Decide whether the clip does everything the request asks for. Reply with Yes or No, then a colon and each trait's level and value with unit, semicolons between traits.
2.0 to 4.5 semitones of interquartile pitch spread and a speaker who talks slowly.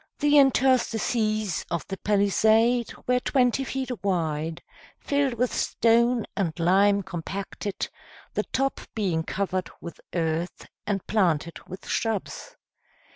No: average, 5.3 semitones; slow, 115 wpm